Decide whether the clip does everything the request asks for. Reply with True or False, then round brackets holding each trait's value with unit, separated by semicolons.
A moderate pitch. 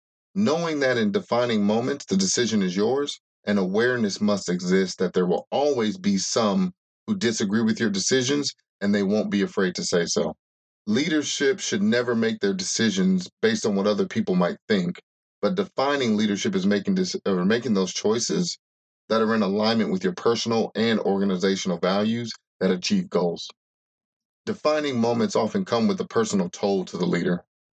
True (145 Hz)